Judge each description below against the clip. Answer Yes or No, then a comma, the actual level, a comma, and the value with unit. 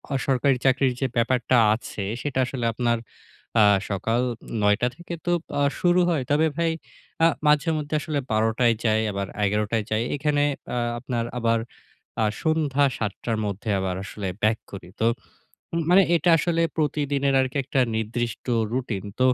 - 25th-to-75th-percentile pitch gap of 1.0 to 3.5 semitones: No, average, 4.8 semitones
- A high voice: No, low, 125 Hz